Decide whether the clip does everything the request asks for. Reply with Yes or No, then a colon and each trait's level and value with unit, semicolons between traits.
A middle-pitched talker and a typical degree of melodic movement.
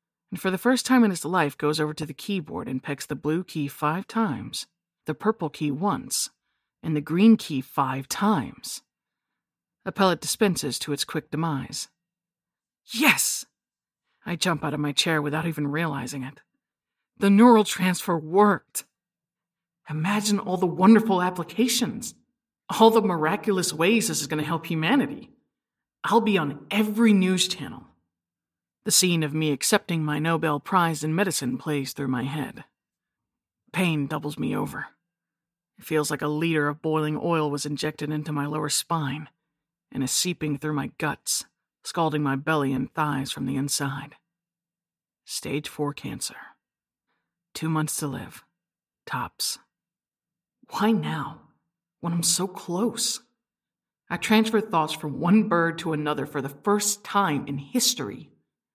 Yes: medium, 165 Hz; average, 4.9 semitones